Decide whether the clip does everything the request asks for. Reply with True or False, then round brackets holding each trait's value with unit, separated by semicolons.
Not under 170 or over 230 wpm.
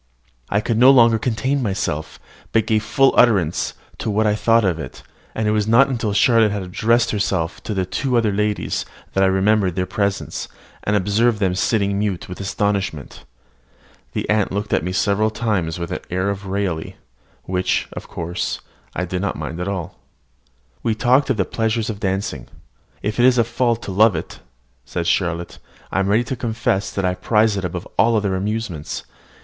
True (190 wpm)